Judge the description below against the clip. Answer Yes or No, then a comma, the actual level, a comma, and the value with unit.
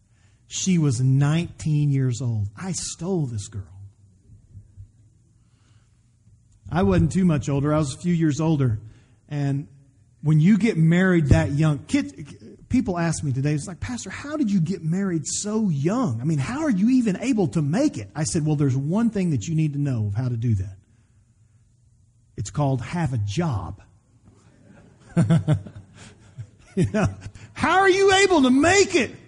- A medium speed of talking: Yes, average, 170 wpm